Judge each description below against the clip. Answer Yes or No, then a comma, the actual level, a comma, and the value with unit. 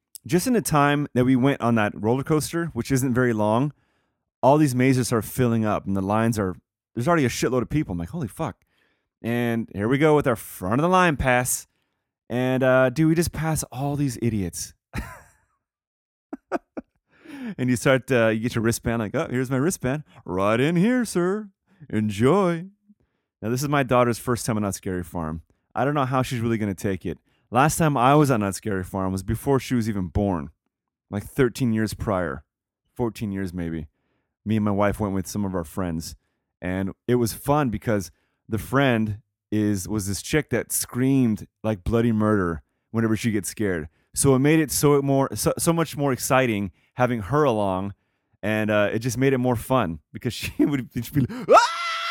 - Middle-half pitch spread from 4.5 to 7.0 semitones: Yes, average, 5.2 semitones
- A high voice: No, low, 120 Hz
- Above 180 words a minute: Yes, average, 200 wpm